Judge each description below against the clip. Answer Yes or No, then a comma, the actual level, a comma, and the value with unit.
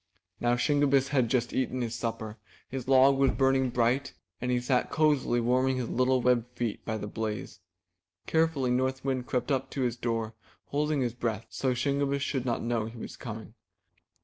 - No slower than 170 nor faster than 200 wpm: Yes, average, 180 wpm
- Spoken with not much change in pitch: Yes, narrow, 2.3 semitones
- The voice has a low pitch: Yes, low, 125 Hz